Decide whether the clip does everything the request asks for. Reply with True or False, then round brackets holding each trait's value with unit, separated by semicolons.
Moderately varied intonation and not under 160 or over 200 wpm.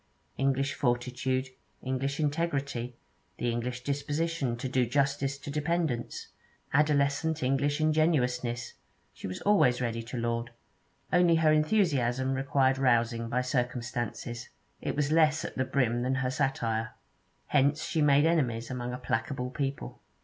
False (3.2 semitones; 135 wpm)